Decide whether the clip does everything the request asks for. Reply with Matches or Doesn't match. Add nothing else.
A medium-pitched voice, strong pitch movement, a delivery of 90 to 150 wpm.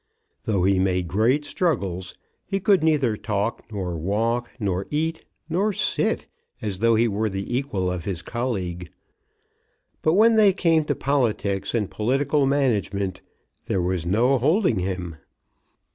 Doesn't match